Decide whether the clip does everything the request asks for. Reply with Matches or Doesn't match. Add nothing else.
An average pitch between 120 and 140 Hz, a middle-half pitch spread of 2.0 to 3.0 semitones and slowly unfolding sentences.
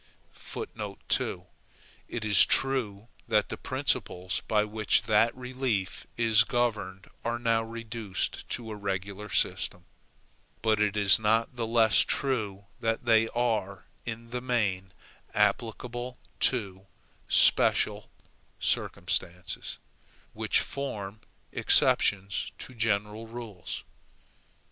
Doesn't match